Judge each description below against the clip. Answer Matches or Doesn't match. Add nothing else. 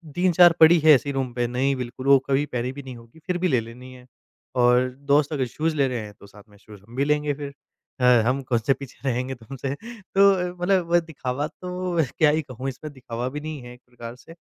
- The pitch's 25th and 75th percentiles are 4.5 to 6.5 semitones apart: Doesn't match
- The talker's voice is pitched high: Doesn't match